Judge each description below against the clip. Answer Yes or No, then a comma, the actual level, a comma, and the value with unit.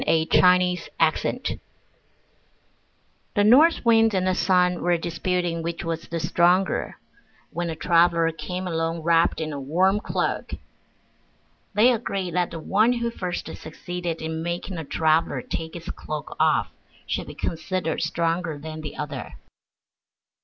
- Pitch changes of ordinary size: No, narrow, 2.1 semitones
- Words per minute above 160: No, average, 140 wpm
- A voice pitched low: No, medium, 170 Hz